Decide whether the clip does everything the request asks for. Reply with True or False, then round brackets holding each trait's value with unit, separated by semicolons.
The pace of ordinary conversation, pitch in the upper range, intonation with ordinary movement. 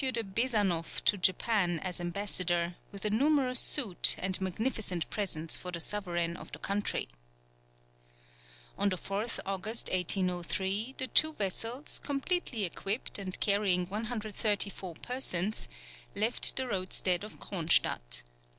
False (125 wpm; 200 Hz; 3.8 semitones)